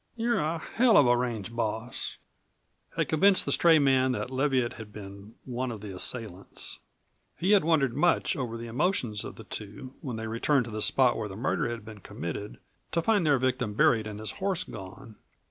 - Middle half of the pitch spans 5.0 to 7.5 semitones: Yes, wide, 5.4 semitones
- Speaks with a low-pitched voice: Yes, low, 120 Hz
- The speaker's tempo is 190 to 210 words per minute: Yes, average, 195 wpm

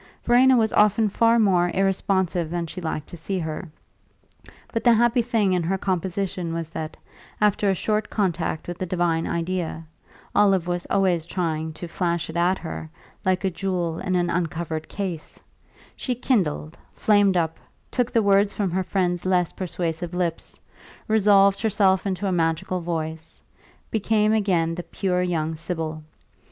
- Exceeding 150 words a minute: Yes, average, 160 wpm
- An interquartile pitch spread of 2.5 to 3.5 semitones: Yes, average, 3.1 semitones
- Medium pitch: Yes, medium, 180 Hz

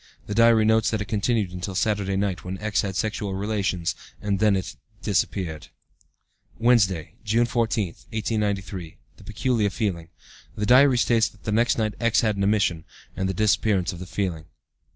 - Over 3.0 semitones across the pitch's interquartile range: No, average, 2.7 semitones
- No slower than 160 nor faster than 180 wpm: Yes, average, 175 wpm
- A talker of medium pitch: No, low, 105 Hz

